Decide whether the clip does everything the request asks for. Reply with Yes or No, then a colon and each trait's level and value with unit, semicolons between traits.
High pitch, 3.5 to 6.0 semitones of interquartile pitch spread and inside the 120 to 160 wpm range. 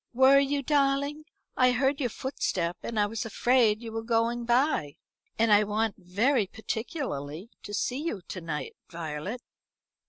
Yes: high, 230 Hz; average, 4.4 semitones; average, 155 wpm